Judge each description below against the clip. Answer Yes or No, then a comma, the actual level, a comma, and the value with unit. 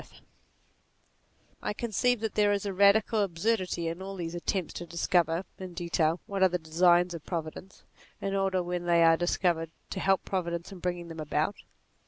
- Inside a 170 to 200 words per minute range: Yes, average, 190 wpm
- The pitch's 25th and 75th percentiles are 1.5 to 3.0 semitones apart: Yes, narrow, 2.5 semitones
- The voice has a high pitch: No, medium, 180 Hz